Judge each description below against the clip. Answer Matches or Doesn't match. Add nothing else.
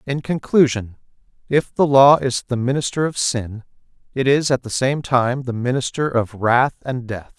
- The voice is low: Matches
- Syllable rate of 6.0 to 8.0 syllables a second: Doesn't match